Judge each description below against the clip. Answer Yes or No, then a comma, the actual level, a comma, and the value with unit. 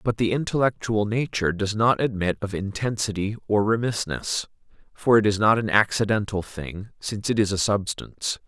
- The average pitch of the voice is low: Yes, low, 105 Hz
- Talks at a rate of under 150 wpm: No, average, 165 wpm